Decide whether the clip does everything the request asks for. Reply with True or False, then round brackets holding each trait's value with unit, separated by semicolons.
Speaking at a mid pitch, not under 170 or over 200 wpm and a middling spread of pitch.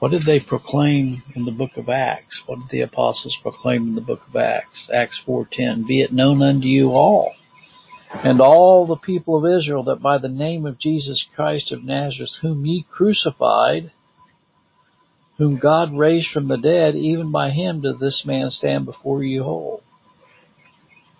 True (145 Hz; 175 wpm; 3.2 semitones)